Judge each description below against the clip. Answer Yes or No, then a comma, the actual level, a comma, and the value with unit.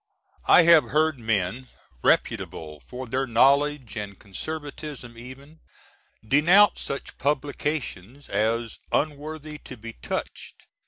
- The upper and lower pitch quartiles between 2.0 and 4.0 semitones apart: No, average, 4.6 semitones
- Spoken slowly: Yes, slow, 105 wpm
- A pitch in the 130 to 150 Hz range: Yes, low, 135 Hz